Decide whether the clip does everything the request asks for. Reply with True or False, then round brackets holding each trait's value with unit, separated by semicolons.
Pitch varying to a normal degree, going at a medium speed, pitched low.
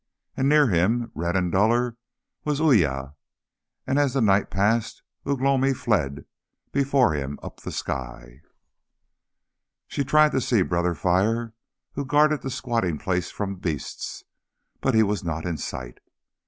False (7.5 semitones; 145 wpm; 105 Hz)